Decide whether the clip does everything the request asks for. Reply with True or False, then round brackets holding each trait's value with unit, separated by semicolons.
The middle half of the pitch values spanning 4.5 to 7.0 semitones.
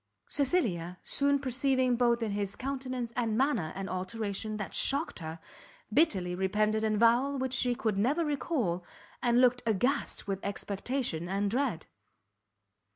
True (5.0 semitones)